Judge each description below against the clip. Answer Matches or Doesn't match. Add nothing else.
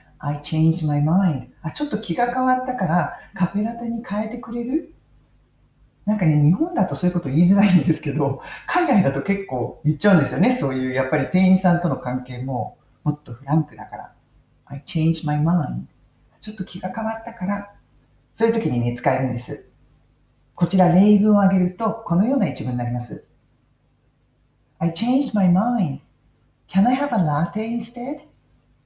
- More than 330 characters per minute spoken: Matches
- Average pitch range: Doesn't match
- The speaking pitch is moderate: Matches